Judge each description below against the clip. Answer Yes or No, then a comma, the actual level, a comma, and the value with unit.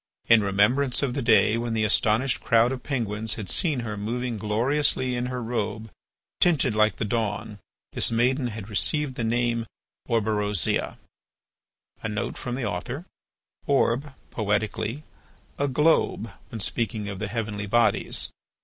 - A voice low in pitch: Yes, low, 115 Hz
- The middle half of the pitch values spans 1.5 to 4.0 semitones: Yes, average, 2.9 semitones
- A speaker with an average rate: No, slow, 130 wpm